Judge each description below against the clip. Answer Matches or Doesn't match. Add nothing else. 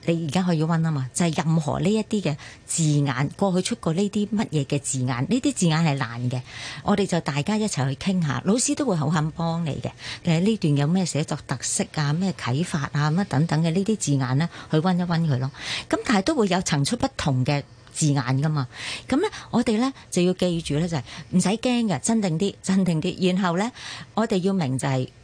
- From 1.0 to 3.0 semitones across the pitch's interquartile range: Doesn't match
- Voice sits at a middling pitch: Matches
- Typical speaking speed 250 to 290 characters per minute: Doesn't match